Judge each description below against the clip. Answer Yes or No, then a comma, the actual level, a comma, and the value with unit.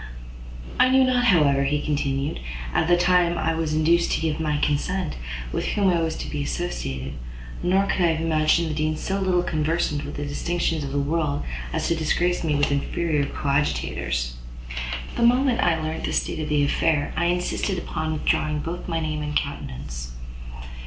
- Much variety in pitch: No, average, 3.2 semitones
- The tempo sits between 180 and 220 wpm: Yes, average, 185 wpm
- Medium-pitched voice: Yes, medium, 155 Hz